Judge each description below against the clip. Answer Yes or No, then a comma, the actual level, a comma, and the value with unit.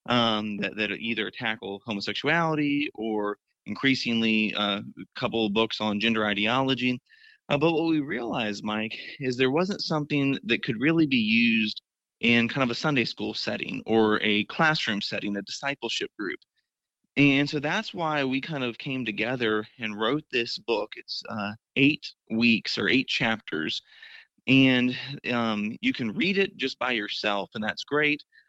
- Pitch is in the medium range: No, low, 125 Hz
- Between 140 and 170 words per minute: Yes, average, 160 wpm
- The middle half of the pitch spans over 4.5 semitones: Yes, average, 5.3 semitones